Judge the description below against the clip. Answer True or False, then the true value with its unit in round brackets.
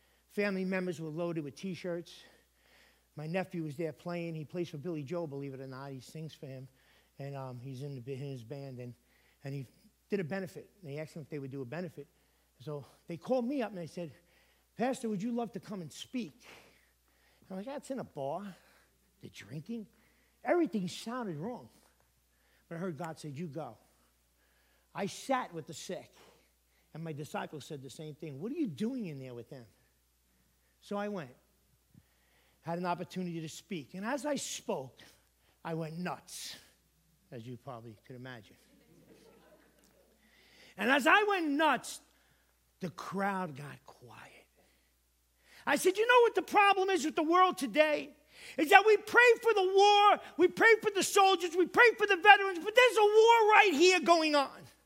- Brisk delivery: False (185 wpm)